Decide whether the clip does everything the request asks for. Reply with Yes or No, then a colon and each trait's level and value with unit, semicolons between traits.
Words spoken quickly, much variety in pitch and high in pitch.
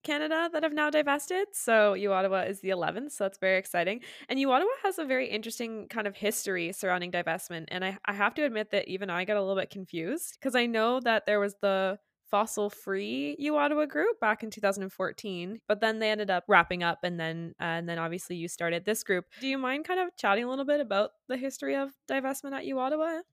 Yes: fast, 240 wpm; wide, 6.1 semitones; high, 210 Hz